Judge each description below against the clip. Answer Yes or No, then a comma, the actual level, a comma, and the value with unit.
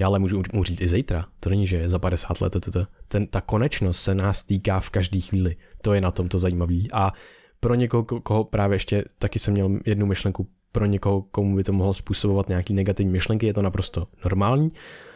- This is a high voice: No, low, 100 Hz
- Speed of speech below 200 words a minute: No, fast, 220 wpm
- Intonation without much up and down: Yes, narrow, 1.8 semitones